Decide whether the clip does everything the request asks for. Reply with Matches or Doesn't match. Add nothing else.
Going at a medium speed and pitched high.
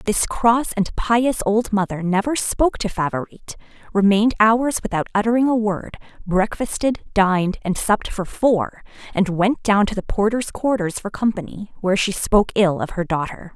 Matches